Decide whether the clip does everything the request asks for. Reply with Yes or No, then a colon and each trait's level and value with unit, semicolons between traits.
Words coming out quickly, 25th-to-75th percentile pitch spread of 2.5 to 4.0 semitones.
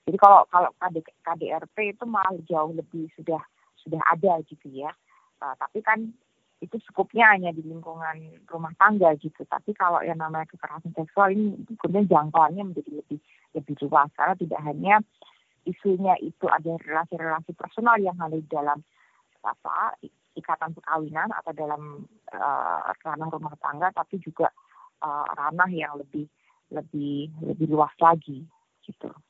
Yes: fast, 145 wpm; average, 3.6 semitones